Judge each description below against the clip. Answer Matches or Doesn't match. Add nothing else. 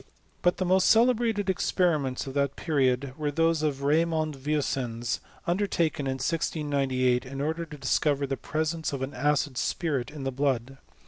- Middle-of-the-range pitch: Matches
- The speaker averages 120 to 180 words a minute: Matches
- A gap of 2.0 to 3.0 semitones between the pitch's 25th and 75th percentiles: Doesn't match